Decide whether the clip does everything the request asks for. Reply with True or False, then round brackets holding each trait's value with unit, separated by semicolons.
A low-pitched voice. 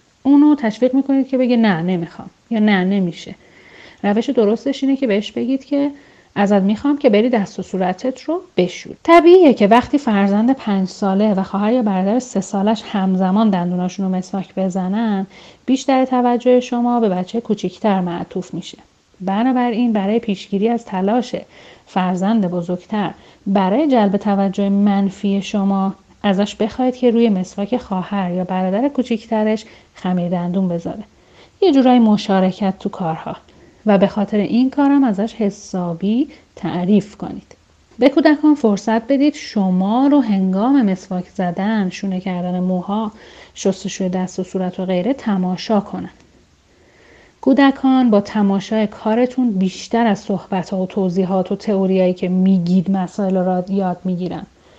False (205 Hz)